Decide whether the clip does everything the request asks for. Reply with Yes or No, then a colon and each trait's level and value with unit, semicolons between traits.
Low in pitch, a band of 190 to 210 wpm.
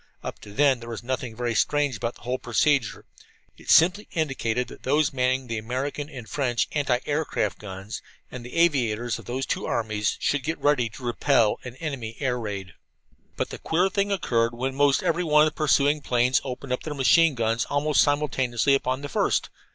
Yes: low, 130 Hz; average, 195 wpm